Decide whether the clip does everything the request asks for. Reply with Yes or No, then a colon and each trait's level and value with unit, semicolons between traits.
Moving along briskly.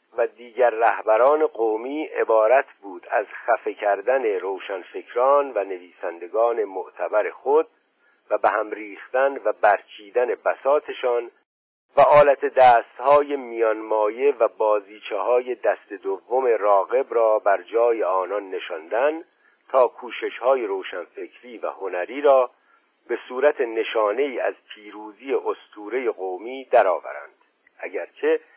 No: average, 110 wpm